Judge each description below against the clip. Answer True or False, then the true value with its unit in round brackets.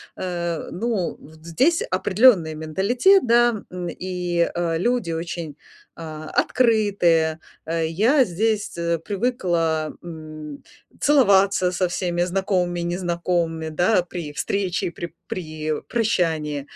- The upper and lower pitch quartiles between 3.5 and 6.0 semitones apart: True (3.8 semitones)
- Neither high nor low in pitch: True (175 Hz)